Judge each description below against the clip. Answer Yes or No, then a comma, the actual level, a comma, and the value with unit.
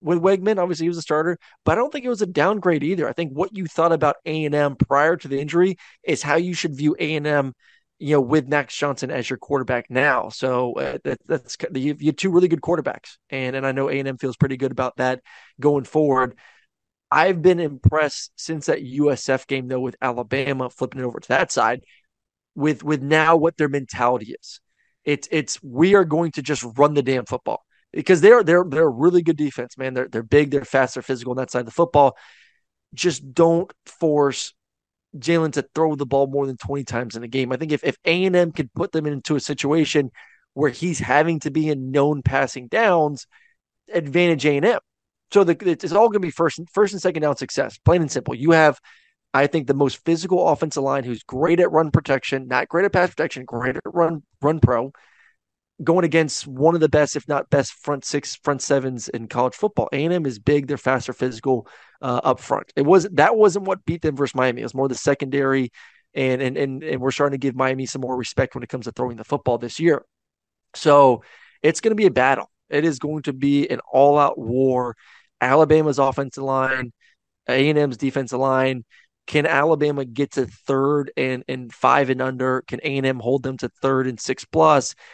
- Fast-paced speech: Yes, fast, 215 wpm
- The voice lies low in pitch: No, medium, 145 Hz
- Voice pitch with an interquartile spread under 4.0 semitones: Yes, average, 3.6 semitones